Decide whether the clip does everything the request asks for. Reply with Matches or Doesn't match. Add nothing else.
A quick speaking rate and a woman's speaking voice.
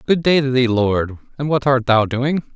Doesn't match